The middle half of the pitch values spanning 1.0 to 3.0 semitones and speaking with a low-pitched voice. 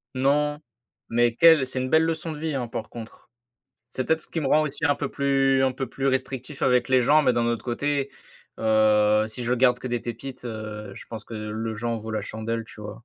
No: average, 3.7 semitones; low, 125 Hz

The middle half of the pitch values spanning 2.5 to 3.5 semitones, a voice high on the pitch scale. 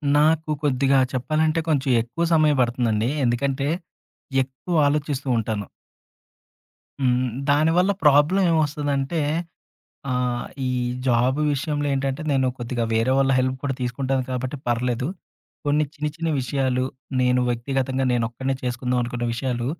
No: average, 2.8 semitones; low, 135 Hz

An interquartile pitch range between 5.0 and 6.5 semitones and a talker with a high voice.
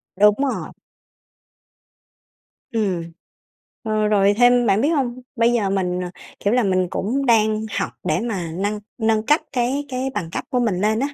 No: average, 3.7 semitones; high, 215 Hz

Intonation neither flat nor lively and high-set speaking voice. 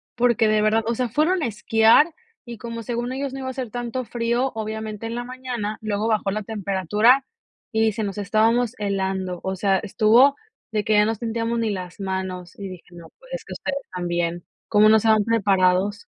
Yes: average, 3.2 semitones; high, 220 Hz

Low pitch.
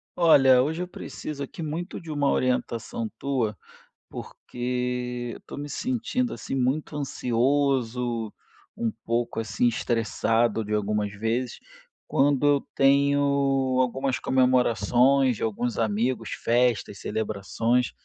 Yes: low, 125 Hz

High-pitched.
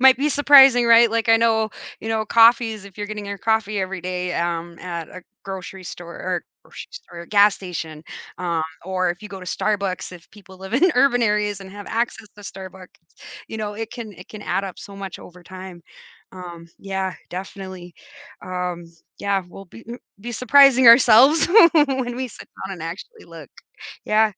Yes: high, 200 Hz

